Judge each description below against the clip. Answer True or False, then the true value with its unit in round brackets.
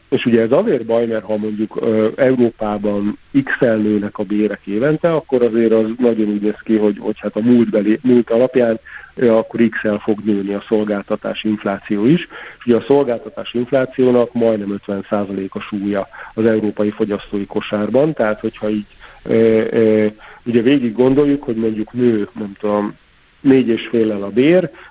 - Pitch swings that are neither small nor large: False (2.3 semitones)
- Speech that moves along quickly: True (160 wpm)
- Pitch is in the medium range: False (110 Hz)